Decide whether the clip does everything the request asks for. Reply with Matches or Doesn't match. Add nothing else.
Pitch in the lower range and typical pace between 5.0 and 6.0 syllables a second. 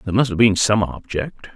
Matches